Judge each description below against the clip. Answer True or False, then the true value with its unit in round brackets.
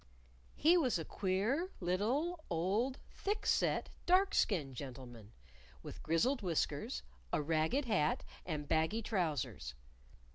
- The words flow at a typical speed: False (115 wpm)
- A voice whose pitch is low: False (185 Hz)